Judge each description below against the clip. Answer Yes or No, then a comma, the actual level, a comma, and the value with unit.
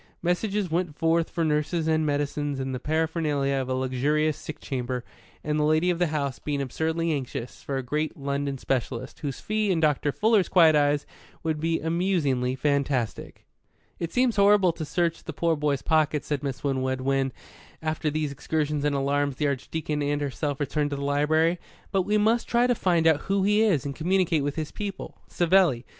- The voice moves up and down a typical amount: Yes, average, 3.1 semitones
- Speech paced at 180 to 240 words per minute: Yes, average, 190 wpm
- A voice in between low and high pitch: Yes, medium, 150 Hz